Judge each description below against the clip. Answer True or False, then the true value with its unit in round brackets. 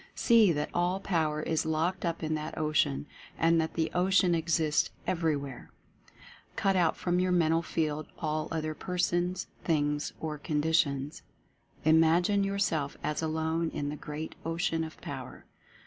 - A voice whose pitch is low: False (160 Hz)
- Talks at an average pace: True (150 wpm)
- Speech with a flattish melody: True (2.3 semitones)